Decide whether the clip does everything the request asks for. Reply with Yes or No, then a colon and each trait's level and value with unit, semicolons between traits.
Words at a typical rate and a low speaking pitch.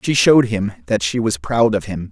No: fast, 255 wpm; low, 105 Hz